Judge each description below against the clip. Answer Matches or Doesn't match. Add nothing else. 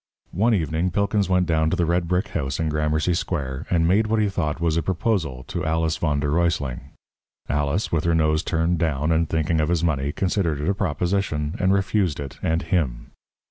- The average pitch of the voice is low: Matches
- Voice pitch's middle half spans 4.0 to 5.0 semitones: Doesn't match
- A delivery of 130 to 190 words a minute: Doesn't match